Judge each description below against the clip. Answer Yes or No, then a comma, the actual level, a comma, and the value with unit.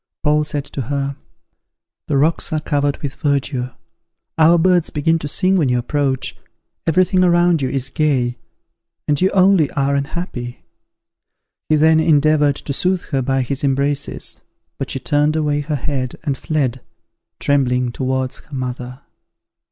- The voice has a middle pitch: Yes, medium, 145 Hz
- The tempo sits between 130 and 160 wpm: Yes, average, 150 wpm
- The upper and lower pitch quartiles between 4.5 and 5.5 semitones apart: No, average, 2.9 semitones